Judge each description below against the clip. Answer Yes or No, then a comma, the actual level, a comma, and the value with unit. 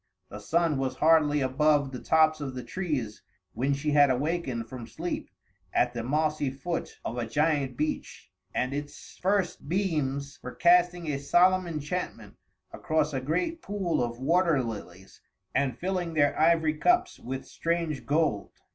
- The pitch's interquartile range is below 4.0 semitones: No, average, 4.4 semitones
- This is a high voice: No, medium, 150 Hz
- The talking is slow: No, average, 155 wpm